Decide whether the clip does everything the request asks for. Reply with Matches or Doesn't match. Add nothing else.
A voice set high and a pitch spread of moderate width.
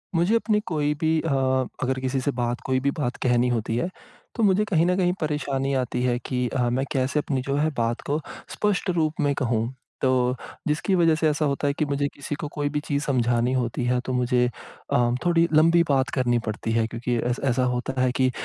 Doesn't match